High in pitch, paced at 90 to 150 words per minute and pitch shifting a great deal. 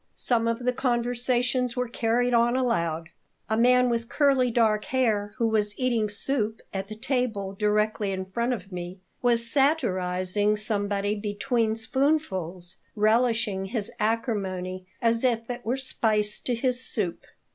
No: high, 225 Hz; average, 145 wpm; average, 3.2 semitones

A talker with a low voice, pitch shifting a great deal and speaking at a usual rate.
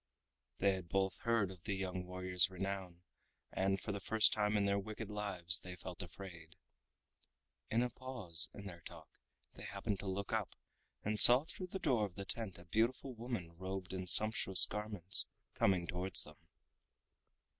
No: very low, 95 Hz; average, 2.9 semitones; average, 170 wpm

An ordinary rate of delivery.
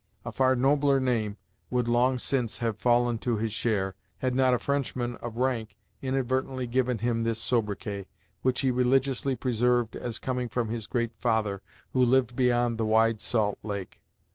Yes: average, 170 wpm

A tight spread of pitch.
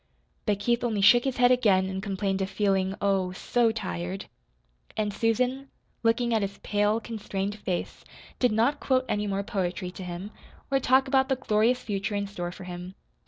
No: average, 3.8 semitones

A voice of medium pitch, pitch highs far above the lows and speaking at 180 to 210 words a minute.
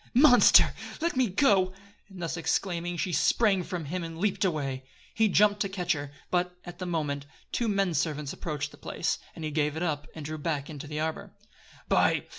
No: medium, 170 Hz; average, 4.1 semitones; average, 200 wpm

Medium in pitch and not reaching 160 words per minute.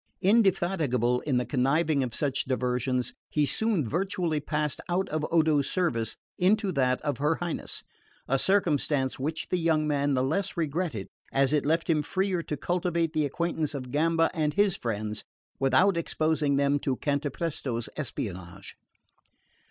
Yes: medium, 150 Hz; average, 150 wpm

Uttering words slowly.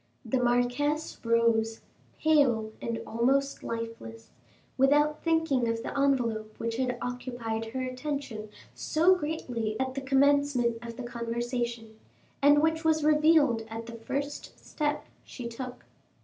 Yes: slow, 130 wpm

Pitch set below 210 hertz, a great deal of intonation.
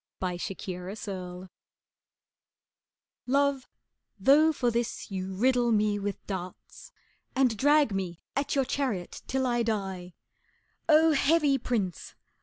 No: high, 225 Hz; wide, 6.2 semitones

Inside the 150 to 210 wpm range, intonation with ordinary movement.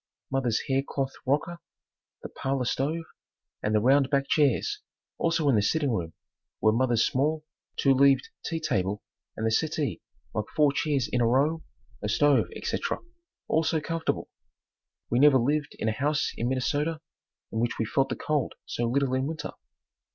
Yes: average, 170 wpm; average, 4.0 semitones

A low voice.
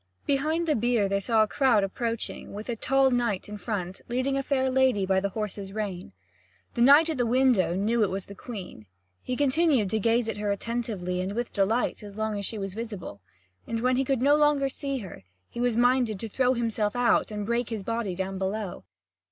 No: high, 225 Hz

